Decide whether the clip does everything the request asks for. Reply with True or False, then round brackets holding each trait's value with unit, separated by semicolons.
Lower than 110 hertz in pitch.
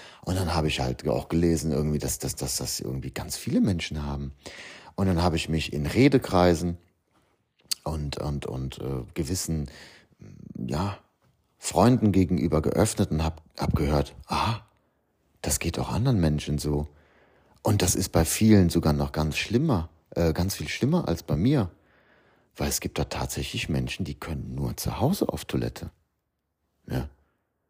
True (80 Hz)